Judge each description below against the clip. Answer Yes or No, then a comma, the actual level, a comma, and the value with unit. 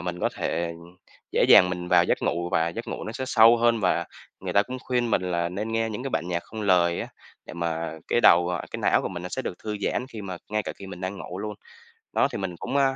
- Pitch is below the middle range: Yes, very low, 95 Hz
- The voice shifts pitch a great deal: No, average, 4.3 semitones